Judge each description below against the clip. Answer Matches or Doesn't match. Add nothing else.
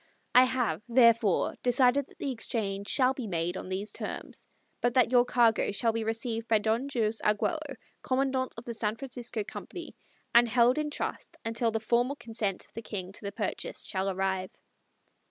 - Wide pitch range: Doesn't match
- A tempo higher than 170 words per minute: Matches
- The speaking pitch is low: Doesn't match